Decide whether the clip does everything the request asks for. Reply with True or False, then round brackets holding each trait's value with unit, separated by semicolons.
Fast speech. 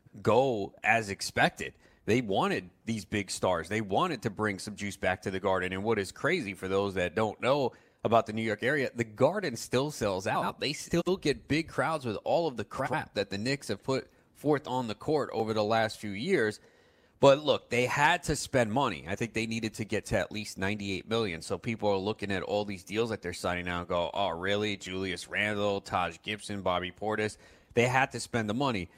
True (220 wpm)